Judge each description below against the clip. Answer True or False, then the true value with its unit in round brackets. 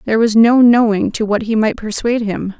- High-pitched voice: True (220 Hz)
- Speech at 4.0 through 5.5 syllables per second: False (5.7 syllables/s)